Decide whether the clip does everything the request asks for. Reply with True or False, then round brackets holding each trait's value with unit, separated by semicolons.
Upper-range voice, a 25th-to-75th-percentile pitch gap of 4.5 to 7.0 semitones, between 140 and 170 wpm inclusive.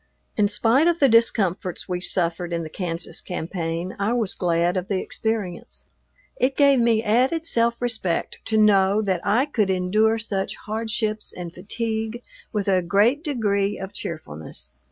False (205 Hz; 4.1 semitones; 155 wpm)